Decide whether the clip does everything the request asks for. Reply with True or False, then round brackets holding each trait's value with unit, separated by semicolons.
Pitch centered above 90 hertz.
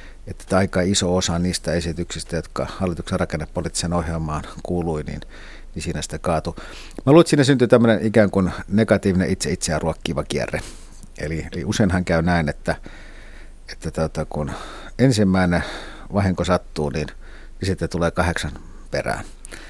False (85 Hz)